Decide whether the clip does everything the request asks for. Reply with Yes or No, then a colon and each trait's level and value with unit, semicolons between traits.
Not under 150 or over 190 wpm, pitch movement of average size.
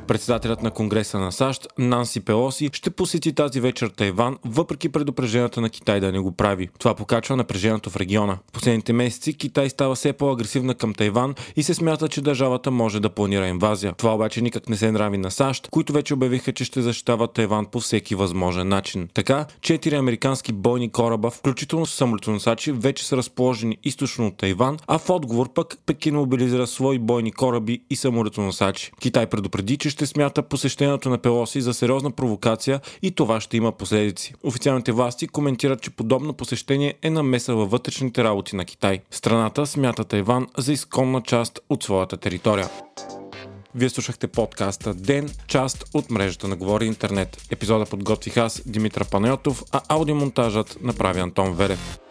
Yes: fast, 165 wpm; average, 4.3 semitones